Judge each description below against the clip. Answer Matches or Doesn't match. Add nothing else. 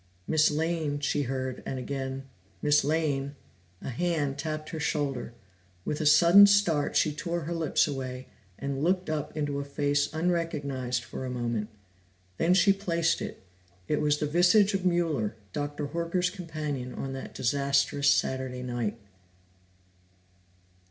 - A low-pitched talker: Doesn't match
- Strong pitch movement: Doesn't match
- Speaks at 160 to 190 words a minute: Doesn't match